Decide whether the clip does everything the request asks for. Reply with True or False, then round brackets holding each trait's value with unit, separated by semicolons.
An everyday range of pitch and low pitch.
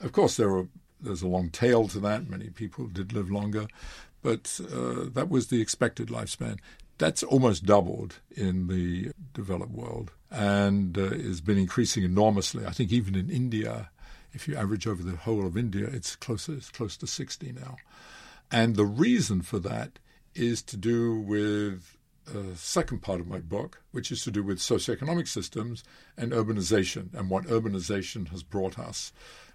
True (3.6 semitones; 105 Hz)